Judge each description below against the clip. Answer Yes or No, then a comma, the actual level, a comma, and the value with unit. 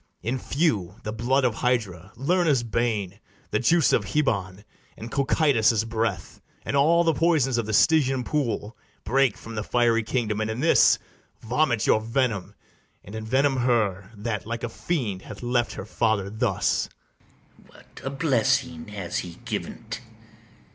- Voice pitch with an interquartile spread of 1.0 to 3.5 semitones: No, average, 4.0 semitones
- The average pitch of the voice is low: Yes, low, 115 Hz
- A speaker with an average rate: Yes, average, 155 wpm